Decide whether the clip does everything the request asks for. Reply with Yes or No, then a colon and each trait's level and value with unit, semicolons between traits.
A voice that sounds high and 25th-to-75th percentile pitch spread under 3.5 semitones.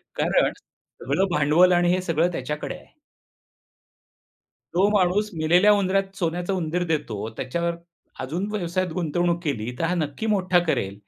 No: medium, 175 Hz; average, 3.1 semitones